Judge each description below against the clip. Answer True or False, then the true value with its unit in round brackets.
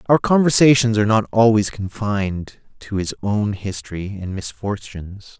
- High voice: False (105 Hz)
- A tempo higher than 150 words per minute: False (135 wpm)